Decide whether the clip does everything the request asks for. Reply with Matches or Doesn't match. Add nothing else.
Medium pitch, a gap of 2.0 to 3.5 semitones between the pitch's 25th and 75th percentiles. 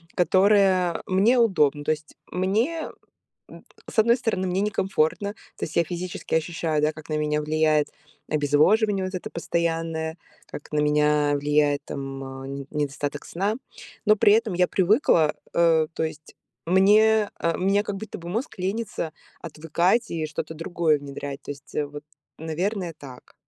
Doesn't match